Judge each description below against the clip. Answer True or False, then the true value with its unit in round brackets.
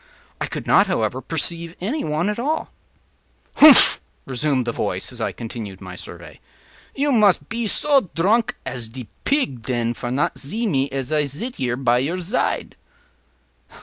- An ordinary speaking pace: True (165 wpm)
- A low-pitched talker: False (150 Hz)